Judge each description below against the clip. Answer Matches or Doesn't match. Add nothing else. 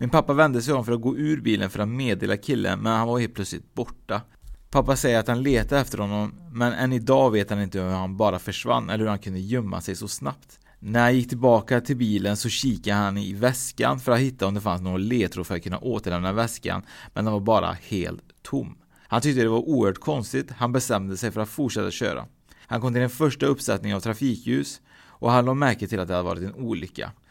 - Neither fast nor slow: Doesn't match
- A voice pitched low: Matches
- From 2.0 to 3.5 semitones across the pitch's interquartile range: Doesn't match